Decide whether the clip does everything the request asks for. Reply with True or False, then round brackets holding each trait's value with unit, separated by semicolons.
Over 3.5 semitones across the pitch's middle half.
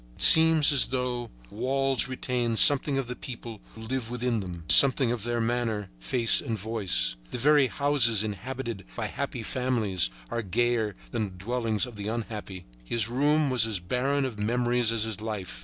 False (3.2 semitones)